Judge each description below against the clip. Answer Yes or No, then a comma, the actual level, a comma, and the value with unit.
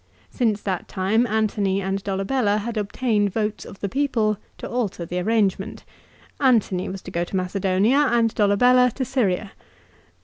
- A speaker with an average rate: Yes, average, 150 wpm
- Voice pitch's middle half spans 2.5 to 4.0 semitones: Yes, average, 3.4 semitones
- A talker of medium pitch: No, high, 210 Hz